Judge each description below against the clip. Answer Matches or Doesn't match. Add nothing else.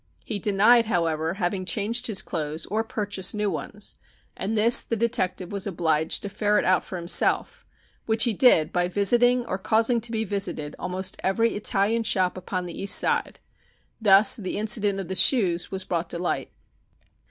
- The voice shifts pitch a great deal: Doesn't match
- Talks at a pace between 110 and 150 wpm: Doesn't match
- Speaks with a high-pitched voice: Matches